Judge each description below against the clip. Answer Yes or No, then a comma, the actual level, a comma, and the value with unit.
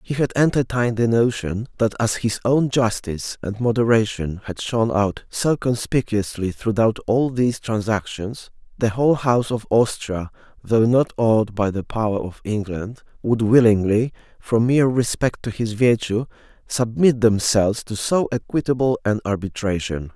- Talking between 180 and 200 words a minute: No, average, 145 wpm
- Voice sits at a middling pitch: No, low, 115 Hz